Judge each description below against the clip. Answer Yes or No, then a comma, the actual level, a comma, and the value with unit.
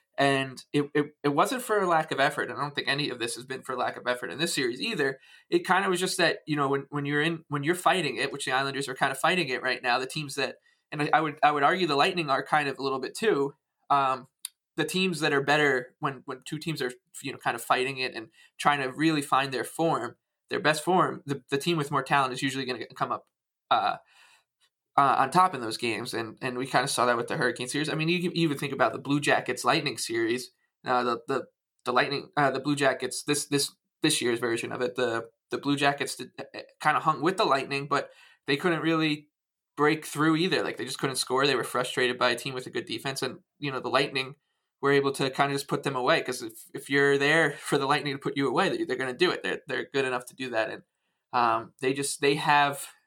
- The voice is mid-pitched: Yes, medium, 145 Hz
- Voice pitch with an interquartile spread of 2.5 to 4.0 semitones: Yes, average, 3.4 semitones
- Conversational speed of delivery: No, fast, 265 wpm